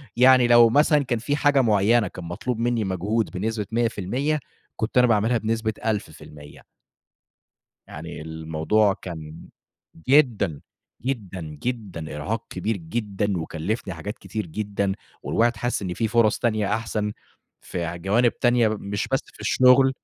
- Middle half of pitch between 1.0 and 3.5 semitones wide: No, average, 4.2 semitones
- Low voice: Yes, low, 110 Hz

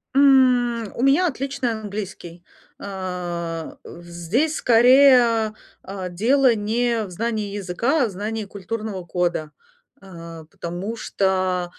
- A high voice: Yes, high, 215 Hz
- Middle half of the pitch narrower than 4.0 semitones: No, average, 5.0 semitones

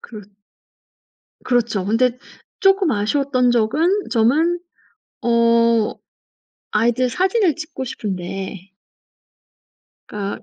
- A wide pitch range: No, average, 4.9 semitones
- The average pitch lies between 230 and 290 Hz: Yes, high, 235 Hz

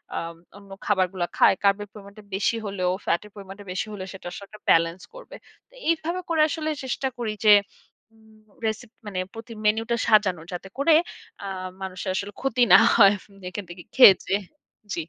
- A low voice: No, high, 205 Hz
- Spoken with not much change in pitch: No, average, 3.1 semitones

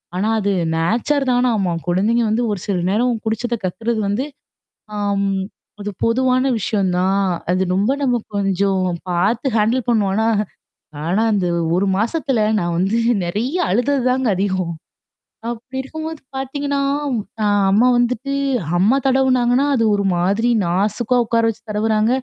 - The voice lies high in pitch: Yes, high, 220 Hz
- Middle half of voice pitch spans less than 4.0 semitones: No, average, 4.3 semitones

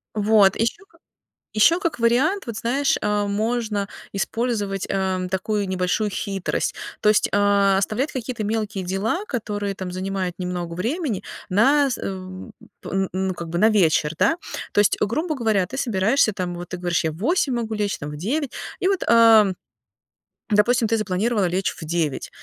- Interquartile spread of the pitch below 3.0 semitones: No, average, 3.8 semitones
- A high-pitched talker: Yes, high, 210 Hz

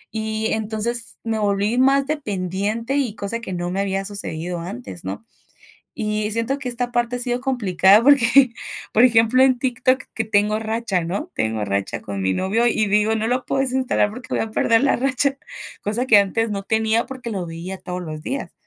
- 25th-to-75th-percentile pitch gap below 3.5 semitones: No, average, 4.1 semitones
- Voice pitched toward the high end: Yes, high, 220 Hz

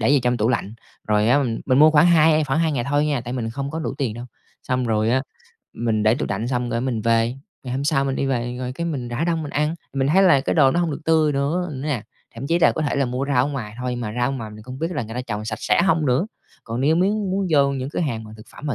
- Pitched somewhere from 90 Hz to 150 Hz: Yes, low, 135 Hz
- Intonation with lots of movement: No, average, 4.3 semitones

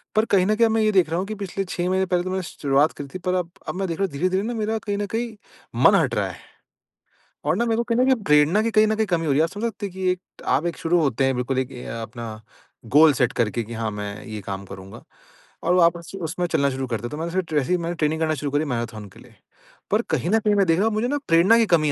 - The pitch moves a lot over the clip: Yes, wide, 6.2 semitones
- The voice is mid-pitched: Yes, medium, 170 Hz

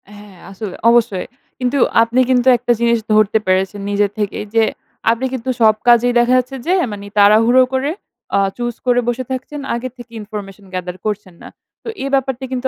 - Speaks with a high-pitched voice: Yes, high, 235 Hz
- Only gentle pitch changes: No, average, 3.5 semitones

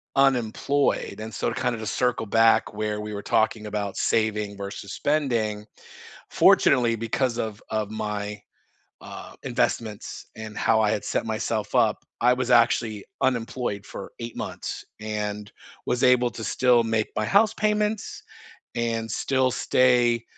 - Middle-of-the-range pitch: No, low, 115 Hz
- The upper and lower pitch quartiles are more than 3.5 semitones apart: No, average, 2.8 semitones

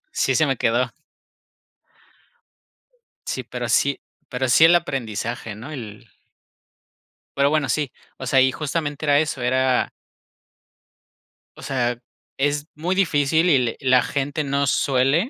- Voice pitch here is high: No, medium, 140 Hz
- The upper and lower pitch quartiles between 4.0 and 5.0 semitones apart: No, average, 3.1 semitones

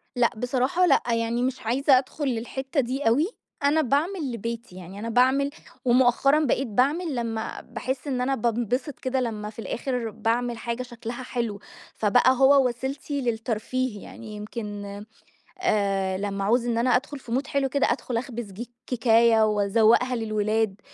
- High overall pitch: Yes, high, 240 Hz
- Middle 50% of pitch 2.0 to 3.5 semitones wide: Yes, average, 2.9 semitones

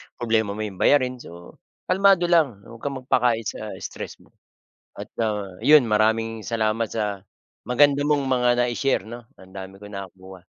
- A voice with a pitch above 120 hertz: No, low, 115 Hz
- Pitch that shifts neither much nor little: Yes, average, 3.8 semitones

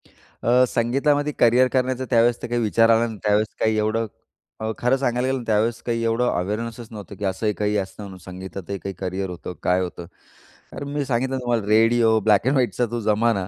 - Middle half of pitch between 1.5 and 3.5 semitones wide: Yes, average, 2.8 semitones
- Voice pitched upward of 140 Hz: No, low, 115 Hz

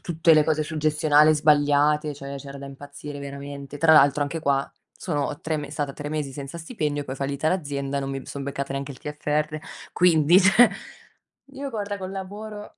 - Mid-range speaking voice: Yes, medium, 150 Hz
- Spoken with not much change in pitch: Yes, narrow, 2.3 semitones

